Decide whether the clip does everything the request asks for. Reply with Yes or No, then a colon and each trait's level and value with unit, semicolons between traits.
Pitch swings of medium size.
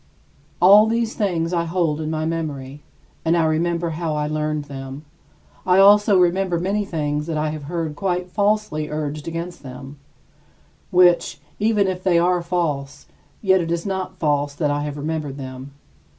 Yes: average, 3.4 semitones